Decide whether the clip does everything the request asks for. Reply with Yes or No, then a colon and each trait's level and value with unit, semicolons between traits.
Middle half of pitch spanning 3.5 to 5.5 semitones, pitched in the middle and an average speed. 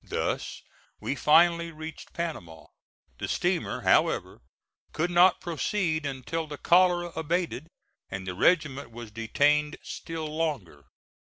No: average, 4.3 semitones; medium, 155 Hz; slow, 115 wpm